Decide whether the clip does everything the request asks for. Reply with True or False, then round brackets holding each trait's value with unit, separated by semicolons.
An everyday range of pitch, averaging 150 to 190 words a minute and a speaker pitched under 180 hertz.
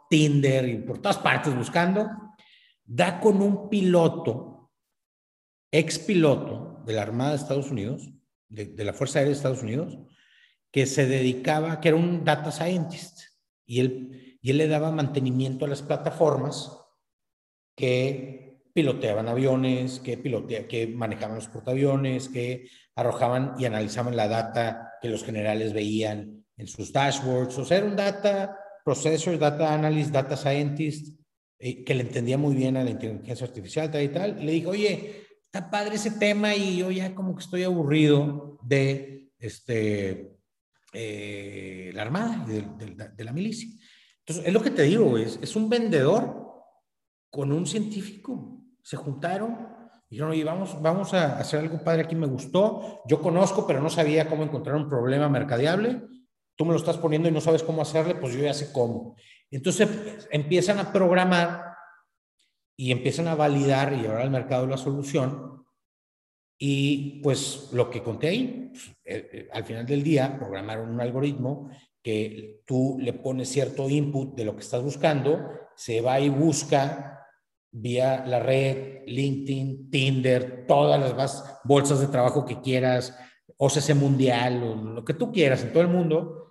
True (4.6 semitones; 160 wpm; 140 Hz)